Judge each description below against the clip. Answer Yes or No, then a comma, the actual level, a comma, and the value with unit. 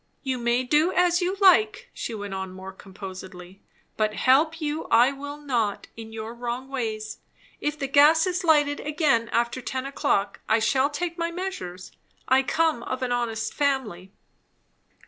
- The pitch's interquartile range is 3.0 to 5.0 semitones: No, wide, 5.4 semitones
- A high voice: Yes, very high, 255 Hz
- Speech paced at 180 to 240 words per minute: No, average, 165 wpm